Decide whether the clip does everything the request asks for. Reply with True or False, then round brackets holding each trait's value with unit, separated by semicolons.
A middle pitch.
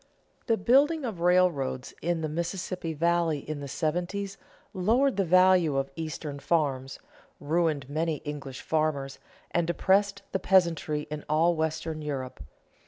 True (165 Hz)